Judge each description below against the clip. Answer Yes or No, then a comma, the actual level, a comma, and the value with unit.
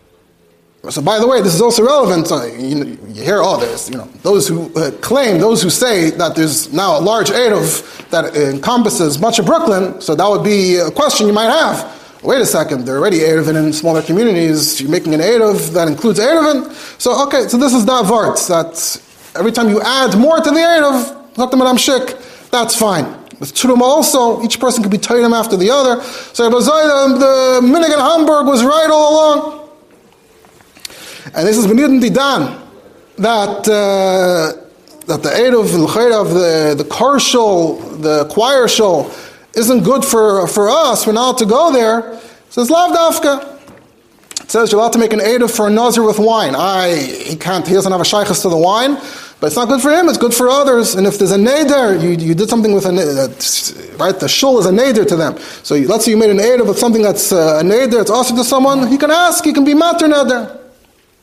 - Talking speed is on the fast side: Yes, fast, 210 wpm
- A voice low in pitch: No, high, 230 Hz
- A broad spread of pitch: Yes, wide, 6.0 semitones